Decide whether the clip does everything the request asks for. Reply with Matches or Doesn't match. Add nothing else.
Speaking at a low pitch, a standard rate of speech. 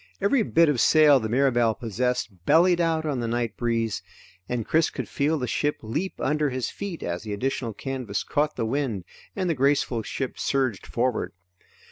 Matches